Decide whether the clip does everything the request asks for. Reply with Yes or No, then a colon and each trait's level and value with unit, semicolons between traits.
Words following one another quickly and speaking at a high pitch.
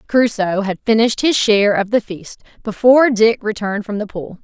No: average, 190 wpm; high, 215 Hz